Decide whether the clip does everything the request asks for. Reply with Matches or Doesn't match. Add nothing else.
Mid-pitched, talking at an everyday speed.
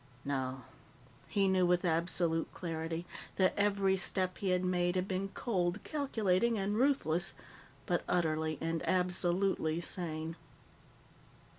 Doesn't match